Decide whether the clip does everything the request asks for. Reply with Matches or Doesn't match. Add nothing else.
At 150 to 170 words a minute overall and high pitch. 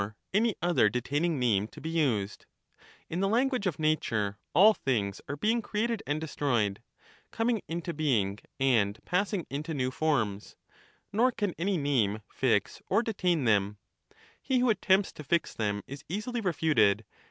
Doesn't match